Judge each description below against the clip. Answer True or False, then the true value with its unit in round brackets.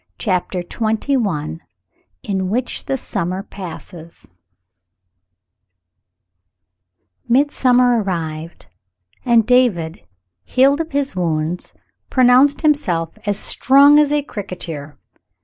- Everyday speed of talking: False (85 wpm)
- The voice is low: False (210 Hz)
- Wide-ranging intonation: True (7.2 semitones)